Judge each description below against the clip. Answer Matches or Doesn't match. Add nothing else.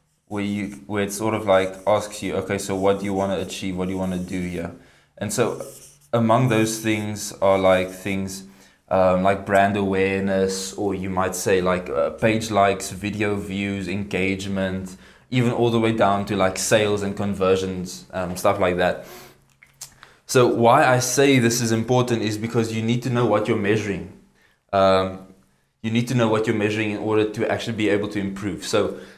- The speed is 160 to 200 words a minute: Matches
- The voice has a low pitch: Matches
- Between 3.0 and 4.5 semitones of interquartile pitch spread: Doesn't match